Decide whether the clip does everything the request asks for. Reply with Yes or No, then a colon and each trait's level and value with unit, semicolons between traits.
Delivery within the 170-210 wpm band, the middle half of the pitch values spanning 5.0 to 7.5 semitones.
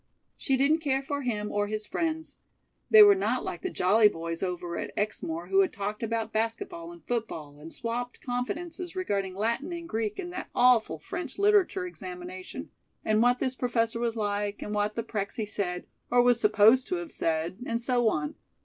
Yes: average, 185 wpm; wide, 5.5 semitones